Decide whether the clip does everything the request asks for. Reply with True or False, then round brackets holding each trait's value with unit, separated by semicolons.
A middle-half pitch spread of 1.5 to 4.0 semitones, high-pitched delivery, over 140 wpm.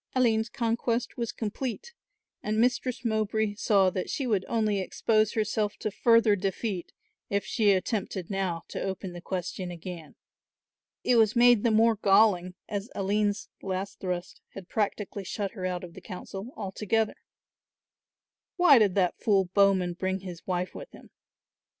True (3.0 semitones; 205 Hz; 150 wpm)